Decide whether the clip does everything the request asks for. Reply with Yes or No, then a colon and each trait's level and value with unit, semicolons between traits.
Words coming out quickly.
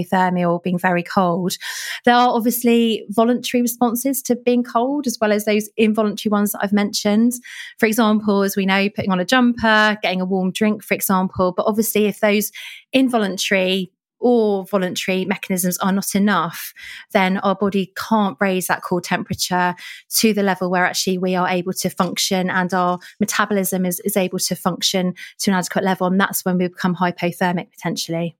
No: average, 180 wpm